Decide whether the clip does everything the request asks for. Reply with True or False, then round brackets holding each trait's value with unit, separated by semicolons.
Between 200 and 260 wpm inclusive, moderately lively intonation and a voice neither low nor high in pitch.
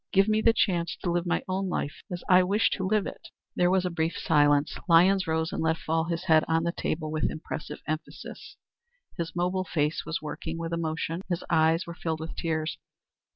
False (205 wpm; 2.1 semitones; 165 Hz)